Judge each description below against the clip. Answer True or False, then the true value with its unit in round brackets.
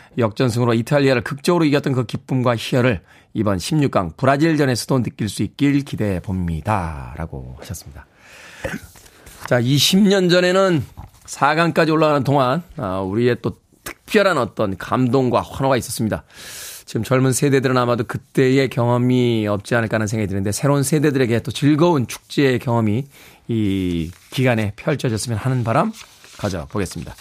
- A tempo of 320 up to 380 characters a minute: True (340 characters per minute)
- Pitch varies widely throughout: False (4.7 semitones)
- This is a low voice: True (125 Hz)